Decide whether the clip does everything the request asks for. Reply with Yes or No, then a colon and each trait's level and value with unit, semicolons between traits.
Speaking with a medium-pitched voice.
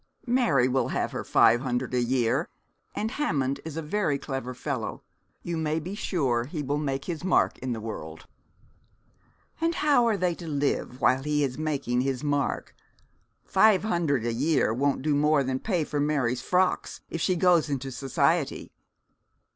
Yes: medium, 145 Hz